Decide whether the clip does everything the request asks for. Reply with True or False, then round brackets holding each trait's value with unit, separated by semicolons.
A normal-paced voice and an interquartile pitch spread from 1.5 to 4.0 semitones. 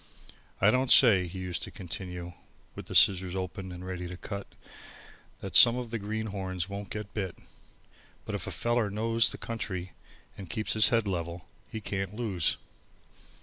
True (170 wpm; 3.2 semitones)